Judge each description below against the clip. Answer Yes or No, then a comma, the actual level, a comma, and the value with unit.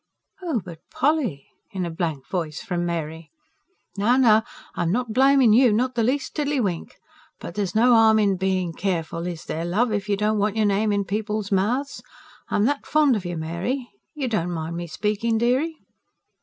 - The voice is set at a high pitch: Yes, high, 210 Hz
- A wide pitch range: Yes, wide, 5.7 semitones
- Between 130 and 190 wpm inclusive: Yes, average, 185 wpm